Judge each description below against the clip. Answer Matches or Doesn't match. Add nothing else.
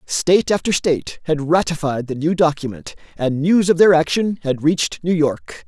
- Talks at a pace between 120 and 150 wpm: Doesn't match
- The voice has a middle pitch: Matches